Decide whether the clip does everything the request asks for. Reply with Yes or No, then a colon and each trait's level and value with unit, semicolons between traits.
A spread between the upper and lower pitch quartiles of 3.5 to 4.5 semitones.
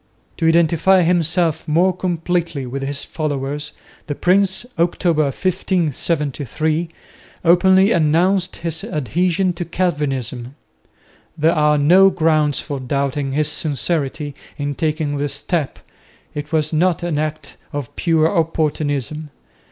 No: average, 3.1 semitones